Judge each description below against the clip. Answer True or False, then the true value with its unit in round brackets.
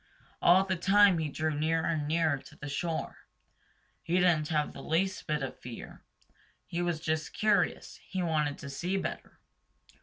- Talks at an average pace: True (170 wpm)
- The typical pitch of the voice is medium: True (160 Hz)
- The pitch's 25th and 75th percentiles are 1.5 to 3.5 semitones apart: True (2.8 semitones)